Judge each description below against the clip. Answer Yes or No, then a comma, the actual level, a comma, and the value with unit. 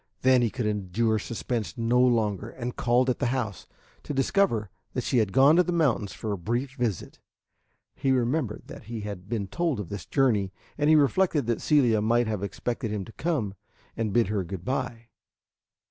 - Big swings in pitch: No, average, 3.8 semitones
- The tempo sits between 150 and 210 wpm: Yes, average, 190 wpm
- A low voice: Yes, low, 115 Hz